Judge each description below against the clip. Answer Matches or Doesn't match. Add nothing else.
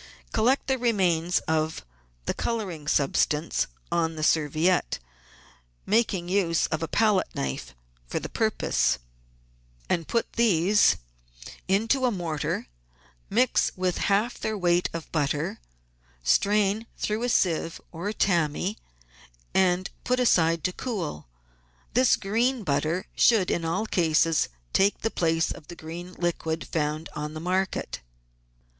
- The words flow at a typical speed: Doesn't match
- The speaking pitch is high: Doesn't match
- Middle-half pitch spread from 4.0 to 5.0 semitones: Matches